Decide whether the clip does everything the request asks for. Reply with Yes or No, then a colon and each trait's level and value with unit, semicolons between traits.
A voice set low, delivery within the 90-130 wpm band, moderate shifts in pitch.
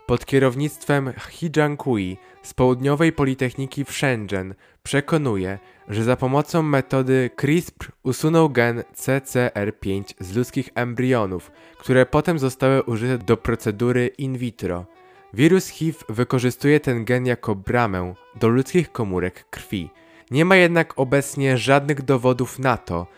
Yes: low, 130 Hz; average, 120 wpm; average, 3.7 semitones